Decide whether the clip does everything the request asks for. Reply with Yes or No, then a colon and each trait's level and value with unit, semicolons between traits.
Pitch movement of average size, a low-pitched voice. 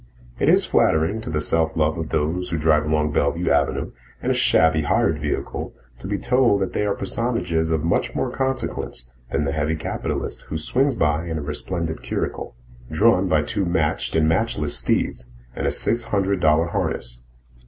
Yes: average, 4.2 semitones; very low, 80 Hz